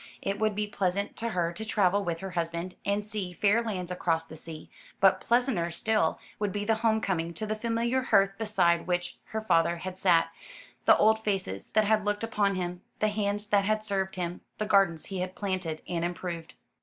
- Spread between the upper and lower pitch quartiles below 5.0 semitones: Yes, average, 3.4 semitones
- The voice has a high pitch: Yes, high, 195 Hz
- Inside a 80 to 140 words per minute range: No, fast, 205 wpm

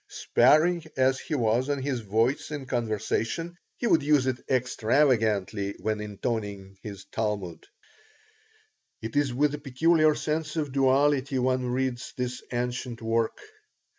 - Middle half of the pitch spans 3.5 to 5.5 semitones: Yes, average, 4.3 semitones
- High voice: No, low, 125 Hz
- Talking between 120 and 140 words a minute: Yes, slow, 135 wpm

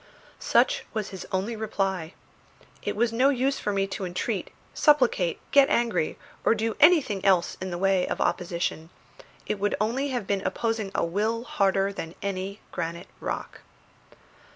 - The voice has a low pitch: No, high, 200 Hz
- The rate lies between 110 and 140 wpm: No, average, 155 wpm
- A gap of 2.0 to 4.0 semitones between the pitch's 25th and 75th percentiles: Yes, average, 3.6 semitones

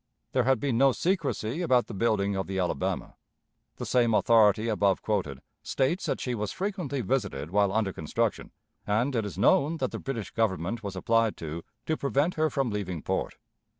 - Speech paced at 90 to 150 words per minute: No, average, 185 wpm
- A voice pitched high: No, low, 110 Hz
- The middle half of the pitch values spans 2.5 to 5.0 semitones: No, wide, 5.4 semitones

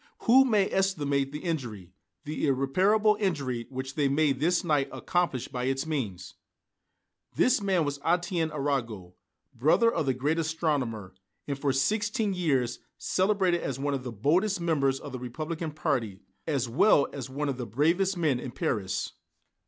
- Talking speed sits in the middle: Yes, average, 160 wpm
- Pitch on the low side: No, medium, 145 Hz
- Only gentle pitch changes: No, average, 4.9 semitones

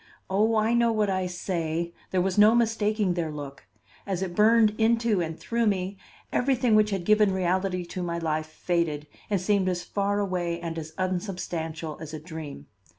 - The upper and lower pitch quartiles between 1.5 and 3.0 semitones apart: No, average, 3.9 semitones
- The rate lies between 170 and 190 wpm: Yes, average, 180 wpm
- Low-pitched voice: No, medium, 185 Hz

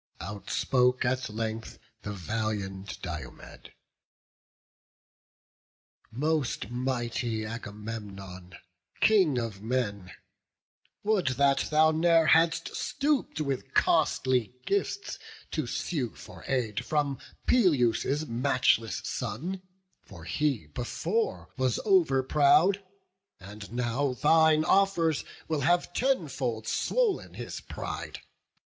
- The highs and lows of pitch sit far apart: Yes, wide, 6.3 semitones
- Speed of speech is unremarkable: No, slow, 95 wpm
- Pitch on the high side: No, low, 130 Hz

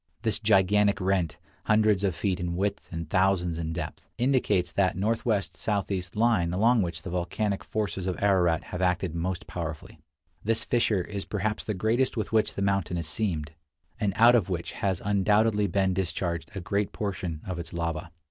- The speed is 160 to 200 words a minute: Yes, average, 175 wpm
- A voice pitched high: No, very low, 95 Hz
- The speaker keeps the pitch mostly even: No, average, 3.2 semitones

